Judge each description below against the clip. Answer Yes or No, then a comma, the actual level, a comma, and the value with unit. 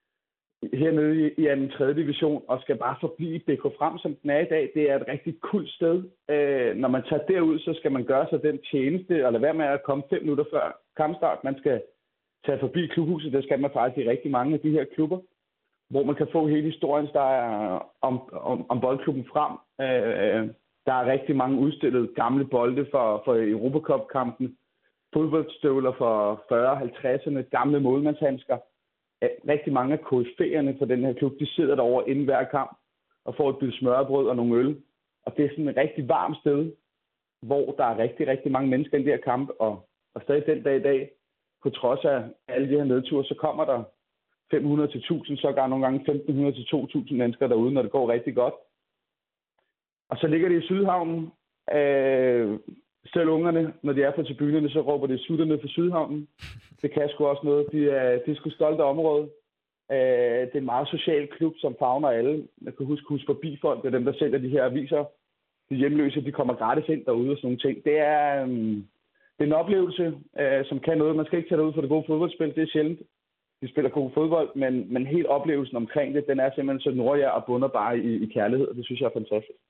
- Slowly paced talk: No, average, 210 wpm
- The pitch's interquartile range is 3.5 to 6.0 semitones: No, average, 2.9 semitones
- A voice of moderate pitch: Yes, medium, 145 Hz